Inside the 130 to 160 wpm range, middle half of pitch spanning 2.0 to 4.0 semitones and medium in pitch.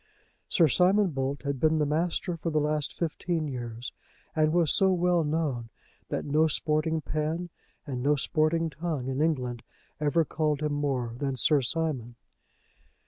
Yes: average, 155 wpm; average, 3.0 semitones; medium, 155 Hz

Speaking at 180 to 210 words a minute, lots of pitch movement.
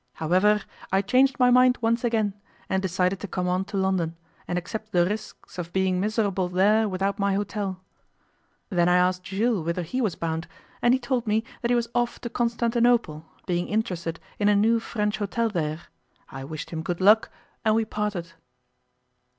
No: average, 185 wpm; average, 3.9 semitones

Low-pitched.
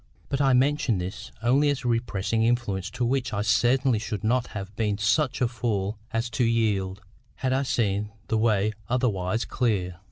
Yes: low, 115 Hz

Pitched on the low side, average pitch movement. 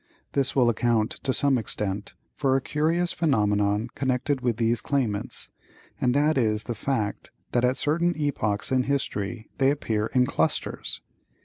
Yes: low, 125 Hz; average, 4.4 semitones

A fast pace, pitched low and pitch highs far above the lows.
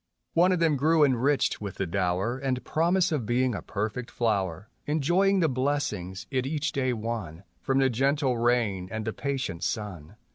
No: average, 185 wpm; low, 125 Hz; wide, 5.7 semitones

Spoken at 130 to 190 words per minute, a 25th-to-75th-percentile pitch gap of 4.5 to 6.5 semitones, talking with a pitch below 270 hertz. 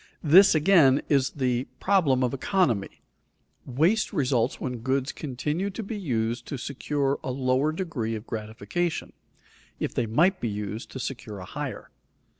Yes: average, 150 wpm; average, 5.2 semitones; low, 135 Hz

